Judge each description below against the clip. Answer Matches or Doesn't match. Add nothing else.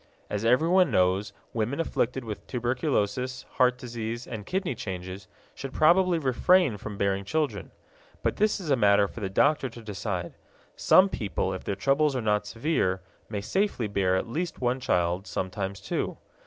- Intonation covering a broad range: Matches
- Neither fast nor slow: Matches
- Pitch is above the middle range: Doesn't match